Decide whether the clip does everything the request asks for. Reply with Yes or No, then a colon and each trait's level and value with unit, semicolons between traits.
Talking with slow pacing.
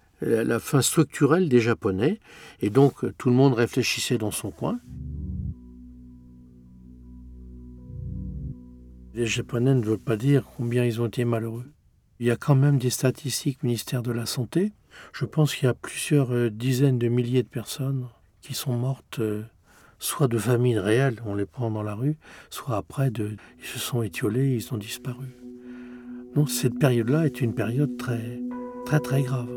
No: average, 165 wpm